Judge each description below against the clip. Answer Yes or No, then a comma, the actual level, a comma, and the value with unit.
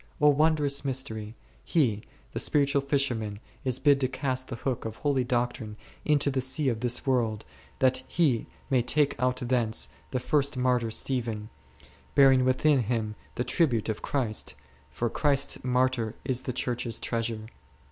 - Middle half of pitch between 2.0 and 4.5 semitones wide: Yes, average, 3.1 semitones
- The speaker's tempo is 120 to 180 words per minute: Yes, average, 155 wpm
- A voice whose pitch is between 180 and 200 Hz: No, low, 125 Hz